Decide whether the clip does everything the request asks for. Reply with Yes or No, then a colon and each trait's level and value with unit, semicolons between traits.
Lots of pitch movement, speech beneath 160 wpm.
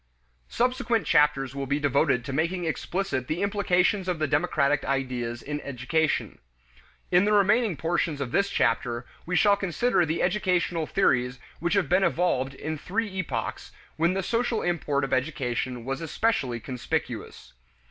Yes: wide, 5.9 semitones; average, 150 wpm